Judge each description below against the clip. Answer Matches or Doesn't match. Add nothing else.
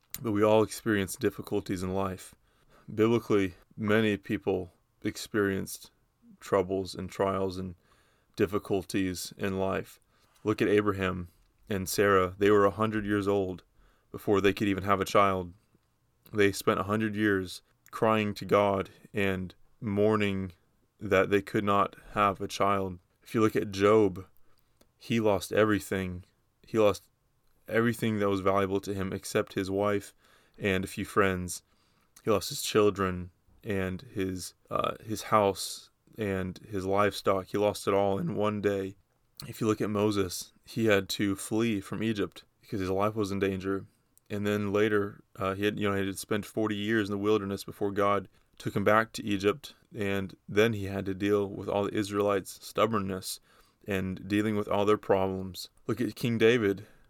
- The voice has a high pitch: Doesn't match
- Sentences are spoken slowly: Doesn't match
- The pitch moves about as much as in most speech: Doesn't match